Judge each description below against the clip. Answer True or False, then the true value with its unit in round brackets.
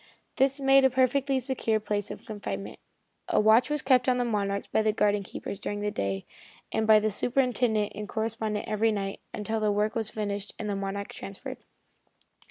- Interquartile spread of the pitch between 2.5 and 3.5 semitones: True (3.2 semitones)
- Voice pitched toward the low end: False (215 Hz)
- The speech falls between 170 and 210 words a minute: True (190 wpm)